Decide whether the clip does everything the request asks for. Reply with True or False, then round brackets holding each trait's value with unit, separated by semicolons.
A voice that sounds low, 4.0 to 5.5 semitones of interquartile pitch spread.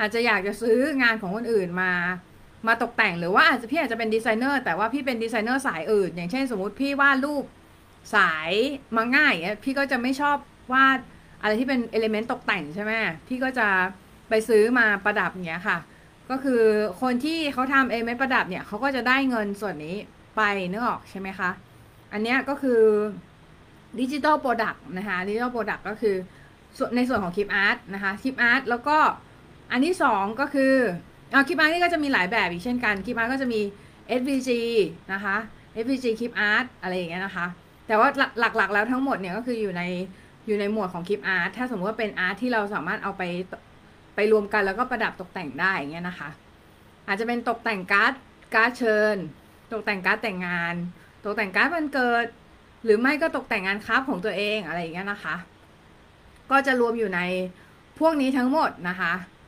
False (220 Hz; 4.4 semitones)